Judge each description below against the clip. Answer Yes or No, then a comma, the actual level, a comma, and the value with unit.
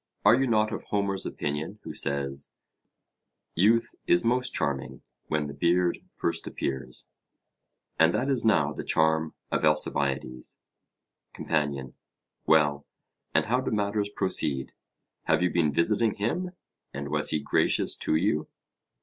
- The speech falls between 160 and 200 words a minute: No, slow, 135 wpm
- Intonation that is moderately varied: No, wide, 6.4 semitones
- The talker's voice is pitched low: Yes, very low, 80 Hz